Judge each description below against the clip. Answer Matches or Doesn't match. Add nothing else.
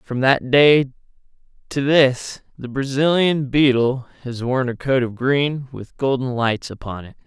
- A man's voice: Matches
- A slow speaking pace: Doesn't match